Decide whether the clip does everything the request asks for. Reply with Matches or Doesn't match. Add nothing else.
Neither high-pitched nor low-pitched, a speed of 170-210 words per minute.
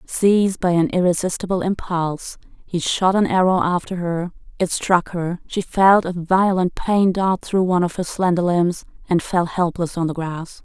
Matches